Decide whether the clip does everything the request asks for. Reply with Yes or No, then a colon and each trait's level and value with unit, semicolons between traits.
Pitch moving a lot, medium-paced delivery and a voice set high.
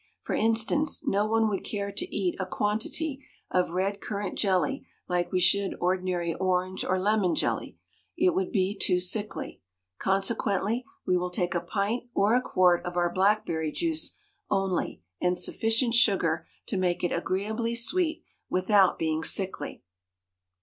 No: average, 3.6 semitones; average, 150 wpm; high, 195 Hz